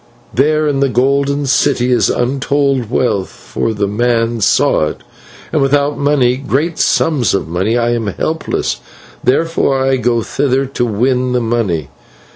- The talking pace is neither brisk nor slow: Yes, average, 150 wpm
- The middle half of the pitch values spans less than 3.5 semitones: Yes, average, 3.1 semitones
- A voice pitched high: No, low, 125 Hz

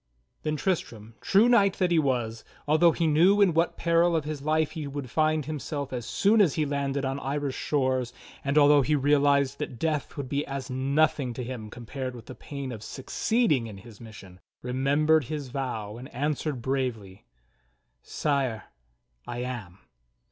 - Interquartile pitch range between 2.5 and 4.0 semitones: Yes, average, 3.6 semitones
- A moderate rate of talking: Yes, average, 175 wpm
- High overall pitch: No, medium, 140 Hz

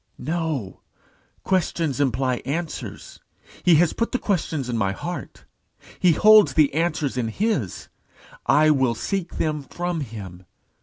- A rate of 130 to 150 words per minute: Yes, slow, 135 wpm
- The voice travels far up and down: Yes, wide, 5.7 semitones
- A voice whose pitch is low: No, medium, 150 Hz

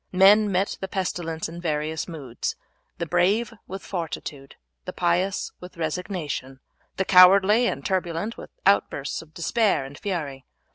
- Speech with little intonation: No, average, 3.4 semitones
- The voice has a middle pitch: Yes, medium, 175 Hz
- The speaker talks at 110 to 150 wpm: Yes, average, 140 wpm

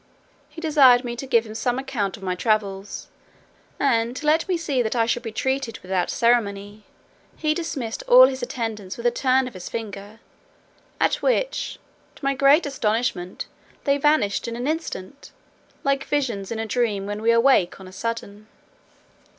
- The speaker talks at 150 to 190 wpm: Yes, average, 175 wpm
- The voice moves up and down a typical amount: Yes, average, 4.6 semitones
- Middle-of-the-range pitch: No, high, 235 Hz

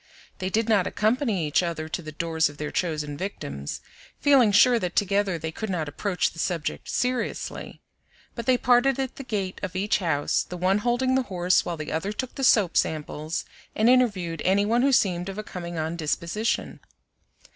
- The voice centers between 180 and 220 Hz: Yes, high, 190 Hz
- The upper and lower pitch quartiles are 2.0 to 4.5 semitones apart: No, wide, 5.6 semitones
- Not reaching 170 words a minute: No, average, 190 wpm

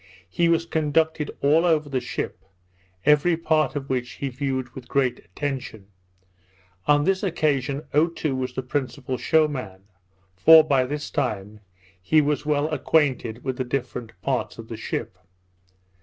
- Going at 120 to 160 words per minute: Yes, average, 150 wpm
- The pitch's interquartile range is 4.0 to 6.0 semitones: No, average, 3.4 semitones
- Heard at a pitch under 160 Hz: Yes, medium, 140 Hz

